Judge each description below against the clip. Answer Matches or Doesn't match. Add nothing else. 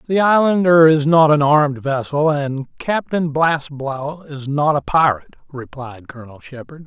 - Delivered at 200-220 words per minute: Doesn't match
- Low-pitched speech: Doesn't match